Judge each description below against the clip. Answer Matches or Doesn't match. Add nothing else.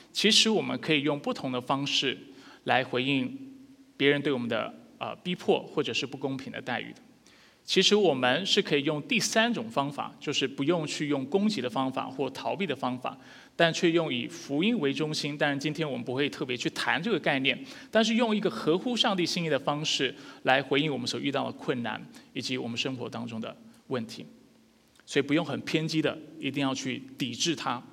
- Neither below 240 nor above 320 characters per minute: Matches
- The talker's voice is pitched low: Doesn't match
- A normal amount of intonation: Matches